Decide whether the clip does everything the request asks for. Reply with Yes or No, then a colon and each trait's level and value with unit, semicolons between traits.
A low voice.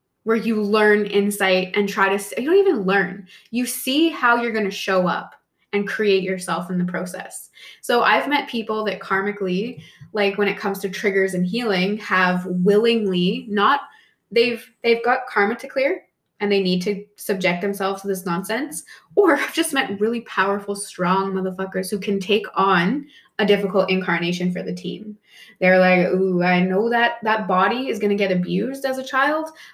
No: high, 200 Hz